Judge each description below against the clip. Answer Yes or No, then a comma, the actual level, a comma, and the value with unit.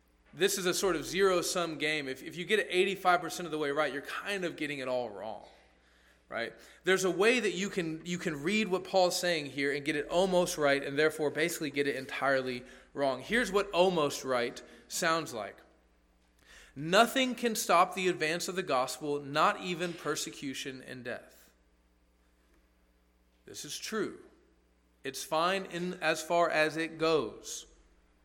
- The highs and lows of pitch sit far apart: Yes, wide, 5.7 semitones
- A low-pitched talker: No, medium, 155 Hz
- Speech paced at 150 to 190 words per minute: Yes, average, 170 wpm